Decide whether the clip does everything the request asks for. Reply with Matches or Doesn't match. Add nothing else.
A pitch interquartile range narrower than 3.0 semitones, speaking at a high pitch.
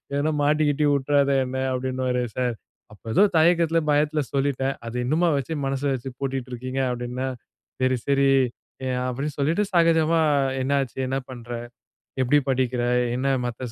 Doesn't match